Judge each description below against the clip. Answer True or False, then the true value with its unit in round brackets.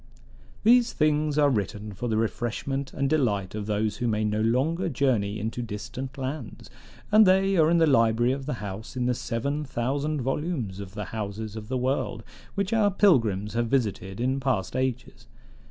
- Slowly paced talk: False (180 wpm)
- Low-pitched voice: True (125 Hz)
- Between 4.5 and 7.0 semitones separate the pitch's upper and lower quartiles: True (5.1 semitones)